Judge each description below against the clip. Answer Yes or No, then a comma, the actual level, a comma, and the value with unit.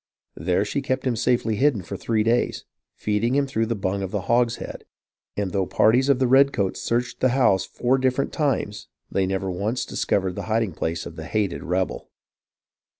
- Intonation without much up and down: No, average, 4.7 semitones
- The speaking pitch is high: No, low, 110 Hz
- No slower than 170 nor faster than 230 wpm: Yes, average, 185 wpm